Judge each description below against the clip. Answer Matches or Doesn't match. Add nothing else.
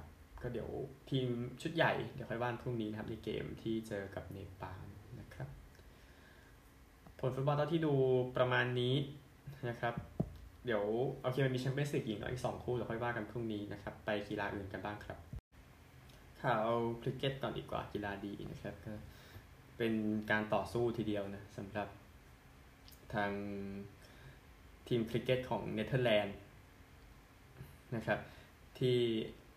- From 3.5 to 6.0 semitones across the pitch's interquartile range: Matches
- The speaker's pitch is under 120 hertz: Matches